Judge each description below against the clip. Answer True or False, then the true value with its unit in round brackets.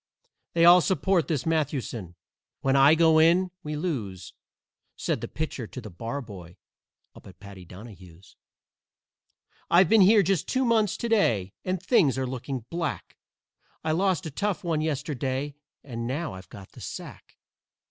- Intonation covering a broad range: True (7.3 semitones)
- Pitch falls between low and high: True (145 Hz)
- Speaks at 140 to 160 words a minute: True (155 wpm)